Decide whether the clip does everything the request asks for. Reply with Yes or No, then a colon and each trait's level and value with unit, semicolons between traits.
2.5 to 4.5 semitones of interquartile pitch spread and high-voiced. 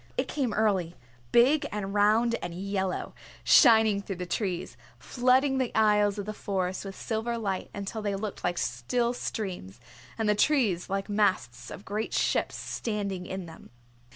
Yes: average, 2.9 semitones; high, 205 Hz